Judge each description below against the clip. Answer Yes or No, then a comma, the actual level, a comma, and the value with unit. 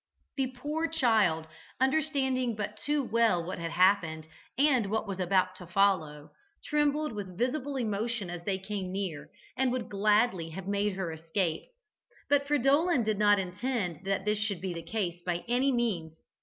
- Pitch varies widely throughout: Yes, wide, 5.9 semitones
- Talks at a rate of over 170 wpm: No, average, 165 wpm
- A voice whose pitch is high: Yes, high, 205 Hz